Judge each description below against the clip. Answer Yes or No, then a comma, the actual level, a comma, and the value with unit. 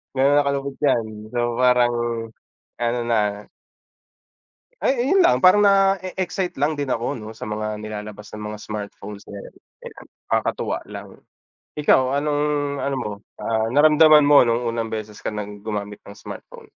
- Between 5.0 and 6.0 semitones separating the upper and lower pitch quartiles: Yes, wide, 5.4 semitones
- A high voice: No, low, 120 Hz